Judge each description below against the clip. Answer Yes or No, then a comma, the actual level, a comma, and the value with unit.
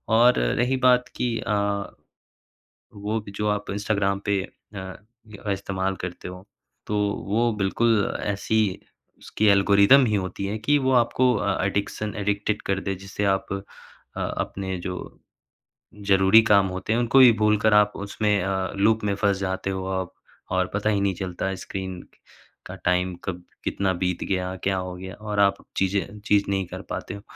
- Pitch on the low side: Yes, low, 100 Hz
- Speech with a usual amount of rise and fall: No, narrow, 1.8 semitones